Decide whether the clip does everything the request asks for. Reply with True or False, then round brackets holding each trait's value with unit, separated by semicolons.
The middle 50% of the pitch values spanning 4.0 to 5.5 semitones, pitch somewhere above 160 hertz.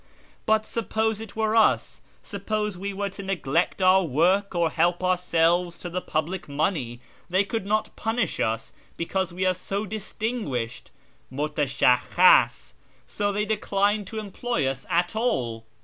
True (4.3 semitones; 185 Hz)